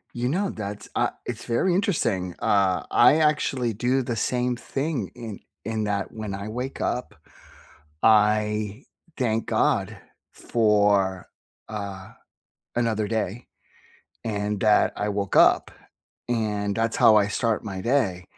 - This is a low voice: Yes, low, 110 Hz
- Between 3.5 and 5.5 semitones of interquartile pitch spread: No, average, 3.0 semitones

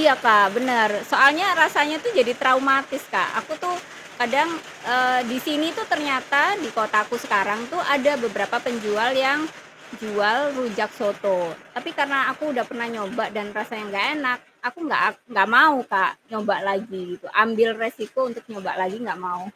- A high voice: Yes, high, 235 Hz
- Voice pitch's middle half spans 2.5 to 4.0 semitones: No, average, 4.6 semitones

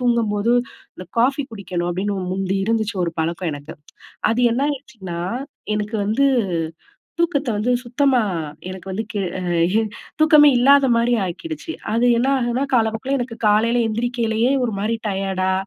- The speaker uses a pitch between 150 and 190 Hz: No, high, 230 Hz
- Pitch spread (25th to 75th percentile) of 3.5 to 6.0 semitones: Yes, average, 4.1 semitones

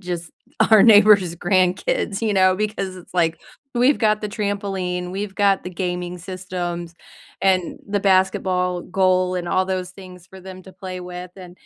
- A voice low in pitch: No, medium, 185 Hz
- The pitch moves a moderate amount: No, narrow, 1.6 semitones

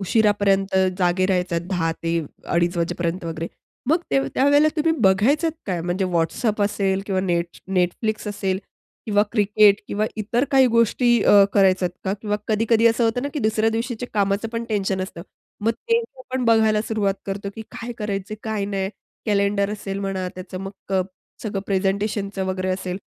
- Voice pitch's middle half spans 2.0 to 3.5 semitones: Yes, average, 2.8 semitones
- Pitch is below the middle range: No, high, 200 Hz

